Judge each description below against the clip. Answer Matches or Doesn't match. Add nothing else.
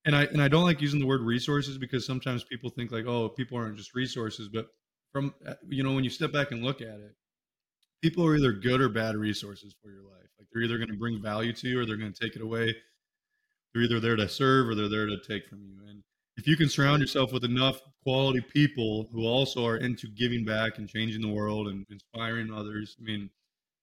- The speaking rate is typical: Doesn't match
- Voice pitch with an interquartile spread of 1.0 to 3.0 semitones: Doesn't match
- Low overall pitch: Matches